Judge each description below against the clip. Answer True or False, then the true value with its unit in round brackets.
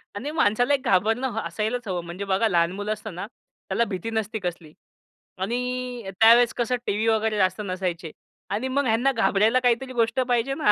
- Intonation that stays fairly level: False (4.0 semitones)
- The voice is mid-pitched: False (220 Hz)